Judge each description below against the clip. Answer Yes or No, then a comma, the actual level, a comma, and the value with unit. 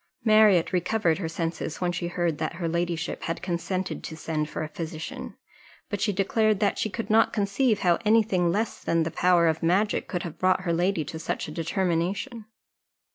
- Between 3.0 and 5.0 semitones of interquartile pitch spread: Yes, average, 3.5 semitones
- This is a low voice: No, medium, 175 Hz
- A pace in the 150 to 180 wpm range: No, average, 195 wpm